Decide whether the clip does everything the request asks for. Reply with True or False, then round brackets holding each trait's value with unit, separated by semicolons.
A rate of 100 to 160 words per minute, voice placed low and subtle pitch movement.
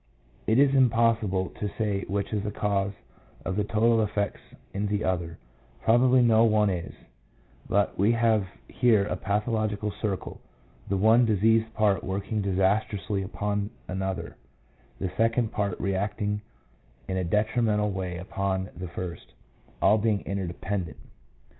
True (140 wpm; 105 Hz; 2.3 semitones)